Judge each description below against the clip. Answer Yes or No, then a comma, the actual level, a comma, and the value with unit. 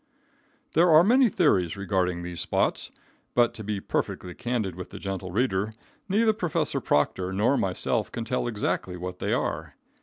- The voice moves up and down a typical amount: No, wide, 6.0 semitones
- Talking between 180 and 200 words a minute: No, average, 160 wpm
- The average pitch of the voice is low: Yes, low, 105 Hz